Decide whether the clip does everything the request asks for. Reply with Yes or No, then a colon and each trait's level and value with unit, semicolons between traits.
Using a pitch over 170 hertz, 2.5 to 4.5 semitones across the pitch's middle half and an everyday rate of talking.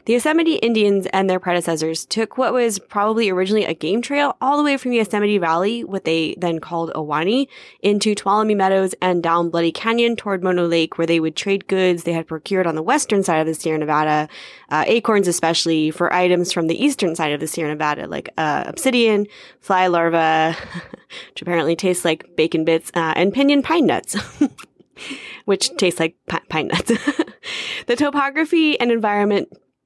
No: high, 190 Hz; wide, 5.5 semitones; average, 185 wpm